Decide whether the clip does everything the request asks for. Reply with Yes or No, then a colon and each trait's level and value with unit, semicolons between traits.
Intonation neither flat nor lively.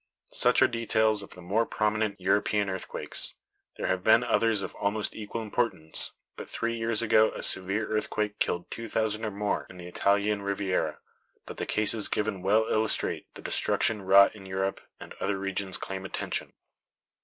No: narrow, 2.1 semitones